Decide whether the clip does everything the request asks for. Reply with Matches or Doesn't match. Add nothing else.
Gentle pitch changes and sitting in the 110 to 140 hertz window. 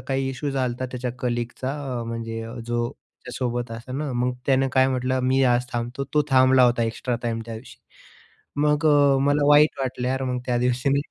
Matches